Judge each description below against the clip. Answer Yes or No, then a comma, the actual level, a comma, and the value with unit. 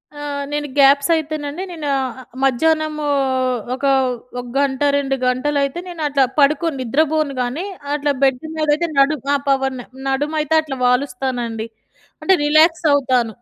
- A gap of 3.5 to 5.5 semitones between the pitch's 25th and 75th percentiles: No, narrow, 2.5 semitones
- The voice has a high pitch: Yes, very high, 285 Hz